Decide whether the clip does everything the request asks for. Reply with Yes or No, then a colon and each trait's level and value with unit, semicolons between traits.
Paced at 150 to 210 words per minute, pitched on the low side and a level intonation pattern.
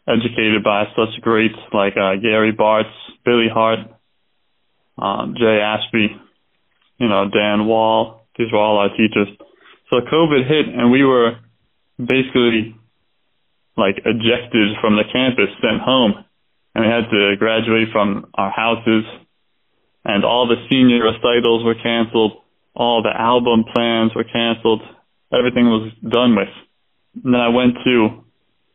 No: average, 140 wpm; low, 115 Hz; narrow, 1.6 semitones